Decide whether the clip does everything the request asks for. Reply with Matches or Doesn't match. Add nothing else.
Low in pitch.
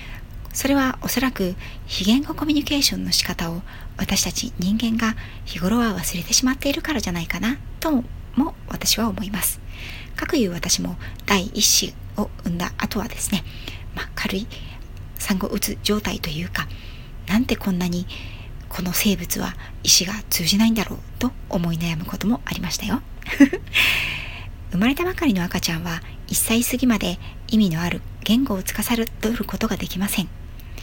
Doesn't match